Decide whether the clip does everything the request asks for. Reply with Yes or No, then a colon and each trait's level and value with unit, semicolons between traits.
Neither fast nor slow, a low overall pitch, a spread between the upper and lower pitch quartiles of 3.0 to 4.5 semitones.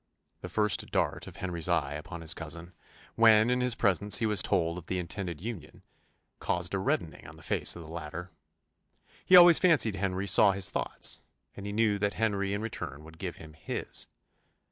Yes: average, 190 wpm; very low, 95 Hz; average, 4.0 semitones